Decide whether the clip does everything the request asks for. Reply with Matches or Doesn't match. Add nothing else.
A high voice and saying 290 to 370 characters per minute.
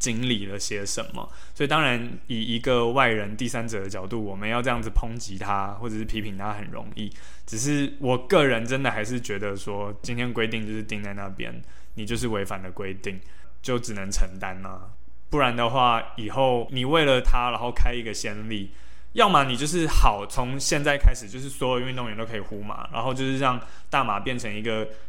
Doesn't match